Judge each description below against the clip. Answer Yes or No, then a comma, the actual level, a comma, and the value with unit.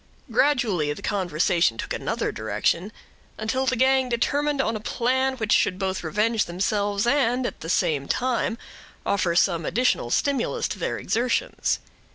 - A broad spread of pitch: Yes, wide, 6.4 semitones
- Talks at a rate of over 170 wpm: No, average, 150 wpm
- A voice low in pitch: No, high, 220 Hz